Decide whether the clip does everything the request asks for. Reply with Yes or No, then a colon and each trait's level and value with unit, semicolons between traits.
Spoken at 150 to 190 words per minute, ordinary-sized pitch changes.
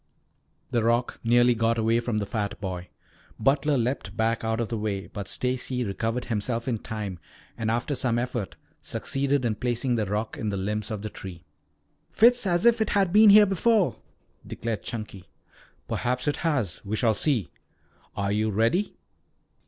Yes: average, 170 wpm; average, 3.4 semitones